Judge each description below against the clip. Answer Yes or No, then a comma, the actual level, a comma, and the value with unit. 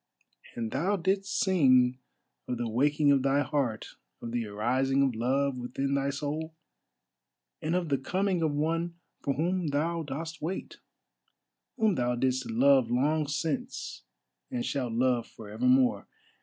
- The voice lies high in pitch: No, medium, 140 Hz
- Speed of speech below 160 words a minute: Yes, average, 150 wpm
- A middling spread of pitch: Yes, average, 4.4 semitones